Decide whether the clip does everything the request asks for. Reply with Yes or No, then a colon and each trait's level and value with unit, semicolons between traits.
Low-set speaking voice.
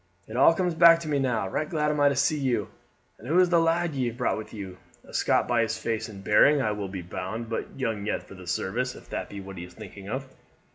Yes: low, 120 Hz